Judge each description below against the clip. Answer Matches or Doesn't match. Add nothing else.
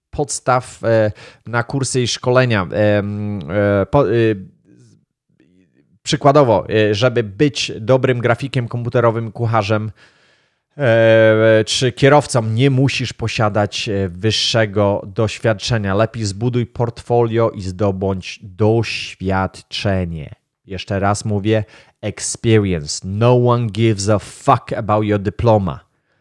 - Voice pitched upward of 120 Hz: Doesn't match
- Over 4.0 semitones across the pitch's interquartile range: Doesn't match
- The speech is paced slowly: Matches